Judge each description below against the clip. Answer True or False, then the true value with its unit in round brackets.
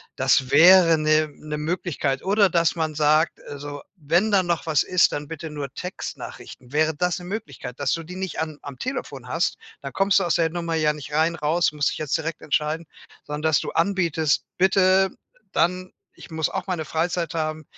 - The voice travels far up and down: False (2.9 semitones)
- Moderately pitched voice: True (160 Hz)